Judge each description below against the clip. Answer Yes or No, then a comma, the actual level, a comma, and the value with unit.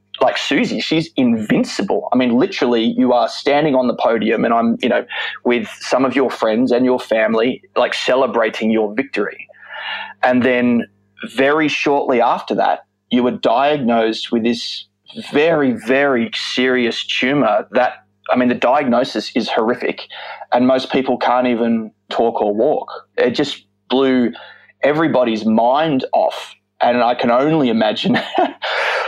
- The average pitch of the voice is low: Yes, low, 120 Hz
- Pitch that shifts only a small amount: Yes, narrow, 2.0 semitones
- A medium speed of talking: Yes, average, 145 wpm